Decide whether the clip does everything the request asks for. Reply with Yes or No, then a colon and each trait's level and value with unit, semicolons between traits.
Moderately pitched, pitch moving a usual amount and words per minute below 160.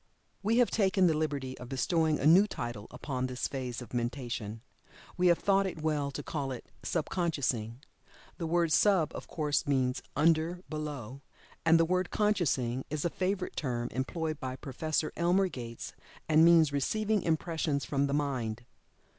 No: medium, 150 Hz; average, 4.8 semitones; average, 165 wpm